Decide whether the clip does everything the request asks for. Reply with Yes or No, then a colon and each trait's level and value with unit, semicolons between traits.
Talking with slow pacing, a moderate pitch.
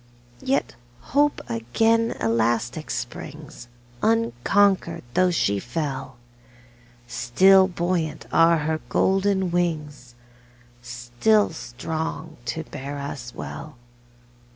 Yes: slow, 85 wpm; medium, 155 Hz